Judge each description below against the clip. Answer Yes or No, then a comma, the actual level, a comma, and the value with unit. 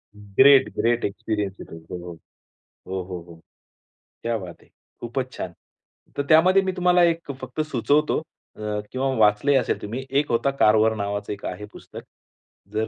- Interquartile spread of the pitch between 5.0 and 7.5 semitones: Yes, wide, 5.5 semitones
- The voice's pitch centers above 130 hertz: No, low, 115 Hz